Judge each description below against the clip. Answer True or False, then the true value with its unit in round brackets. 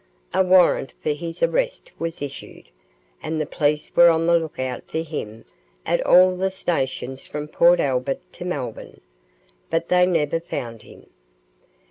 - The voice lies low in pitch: False (165 Hz)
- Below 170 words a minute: True (155 wpm)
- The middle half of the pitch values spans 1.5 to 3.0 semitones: False (3.7 semitones)